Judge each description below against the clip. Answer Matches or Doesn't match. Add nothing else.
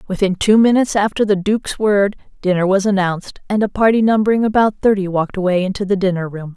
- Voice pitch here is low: Doesn't match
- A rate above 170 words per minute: Matches